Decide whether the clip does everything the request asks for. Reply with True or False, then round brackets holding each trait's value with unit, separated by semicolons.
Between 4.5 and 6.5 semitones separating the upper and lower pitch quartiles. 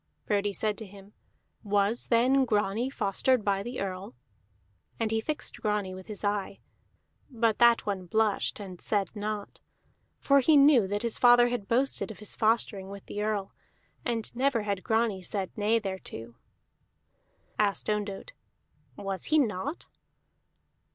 False (3.0 semitones)